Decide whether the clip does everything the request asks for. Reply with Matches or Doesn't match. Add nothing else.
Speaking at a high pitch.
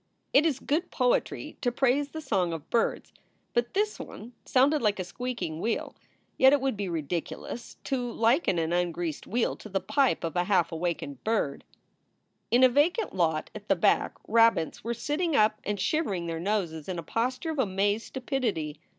Matches